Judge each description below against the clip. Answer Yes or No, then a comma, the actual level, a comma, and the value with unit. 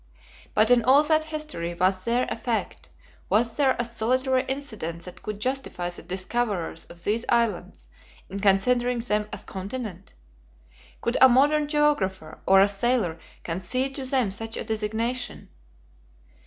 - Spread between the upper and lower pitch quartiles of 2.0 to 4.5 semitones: No, average, 5.1 semitones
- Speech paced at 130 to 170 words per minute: Yes, average, 150 wpm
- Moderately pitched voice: No, high, 230 Hz